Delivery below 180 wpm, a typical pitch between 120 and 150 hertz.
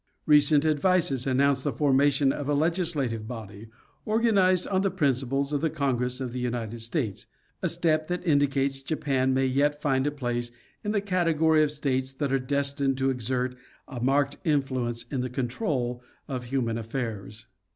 Yes: average, 165 wpm; low, 135 Hz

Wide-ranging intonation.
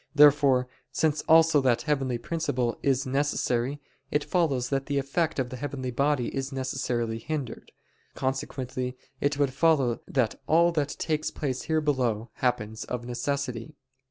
No: average, 2.8 semitones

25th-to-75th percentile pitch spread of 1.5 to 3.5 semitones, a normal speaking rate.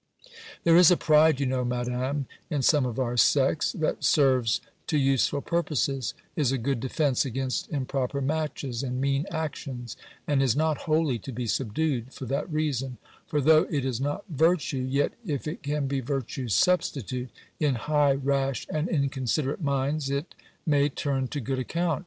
Yes: average, 2.7 semitones; average, 170 wpm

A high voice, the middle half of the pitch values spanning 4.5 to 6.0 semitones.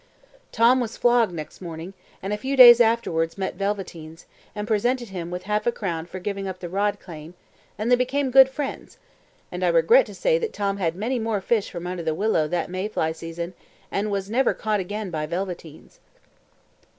Yes: high, 200 Hz; average, 5.1 semitones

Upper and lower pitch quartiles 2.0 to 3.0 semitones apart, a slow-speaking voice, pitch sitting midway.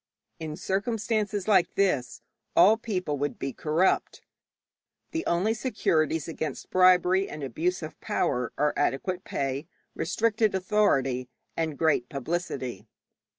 No: average, 5.3 semitones; slow, 115 wpm; medium, 170 Hz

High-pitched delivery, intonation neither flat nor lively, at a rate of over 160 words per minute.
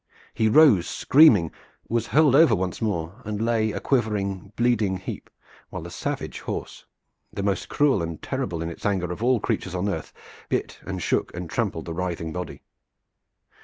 No: low, 100 Hz; average, 4.9 semitones; average, 170 wpm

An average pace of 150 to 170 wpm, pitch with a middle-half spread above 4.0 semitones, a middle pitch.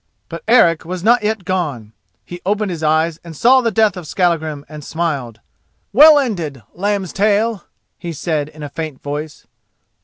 Yes: average, 160 wpm; average, 5.3 semitones; medium, 170 Hz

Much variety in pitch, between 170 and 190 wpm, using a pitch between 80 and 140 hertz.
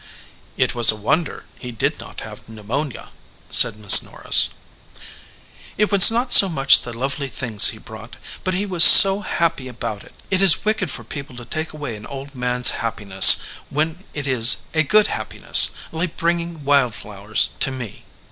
Yes: wide, 6.5 semitones; average, 175 wpm; low, 135 Hz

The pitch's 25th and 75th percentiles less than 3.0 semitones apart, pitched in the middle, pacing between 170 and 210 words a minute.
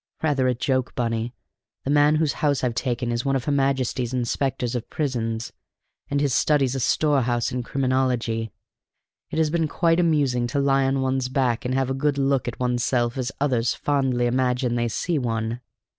No: narrow, 2.5 semitones; low, 130 Hz; average, 190 wpm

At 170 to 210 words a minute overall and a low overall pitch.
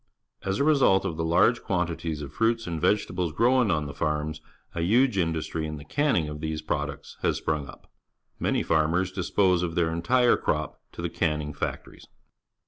Yes: average, 180 wpm; very low, 85 Hz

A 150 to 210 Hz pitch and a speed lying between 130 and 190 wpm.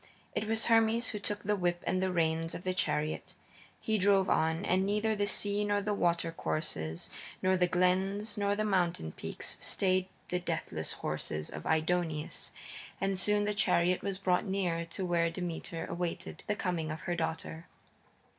Yes: medium, 185 Hz; average, 175 wpm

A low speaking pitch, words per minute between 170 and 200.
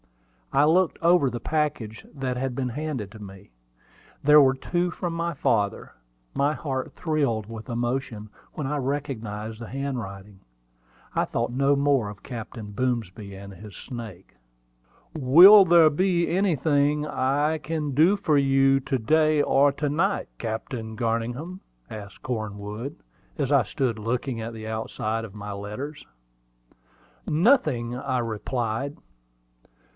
No: low, 130 Hz; slow, 135 wpm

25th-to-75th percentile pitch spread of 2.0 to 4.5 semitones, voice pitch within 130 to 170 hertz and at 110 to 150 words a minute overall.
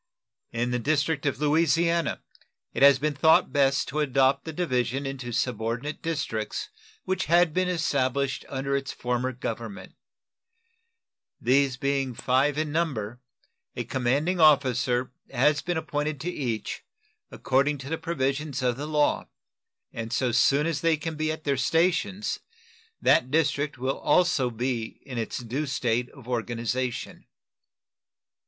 Yes: average, 3.6 semitones; medium, 140 Hz; average, 140 wpm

